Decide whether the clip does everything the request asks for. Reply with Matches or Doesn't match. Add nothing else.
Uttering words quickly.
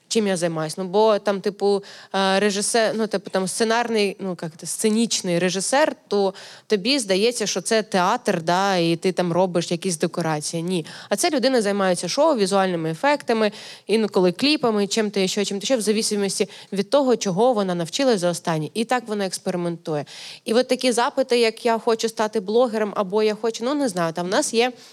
Matches